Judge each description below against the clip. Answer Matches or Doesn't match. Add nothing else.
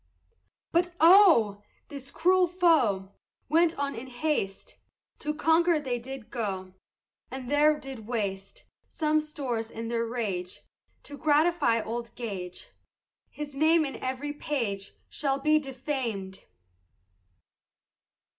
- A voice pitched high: Matches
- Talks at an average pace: Doesn't match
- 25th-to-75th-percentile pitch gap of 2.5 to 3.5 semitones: Doesn't match